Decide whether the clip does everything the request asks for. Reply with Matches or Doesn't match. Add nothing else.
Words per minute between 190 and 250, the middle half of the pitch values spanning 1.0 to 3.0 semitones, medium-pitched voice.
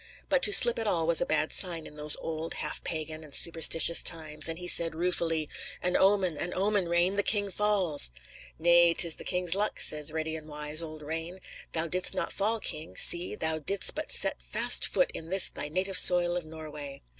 Matches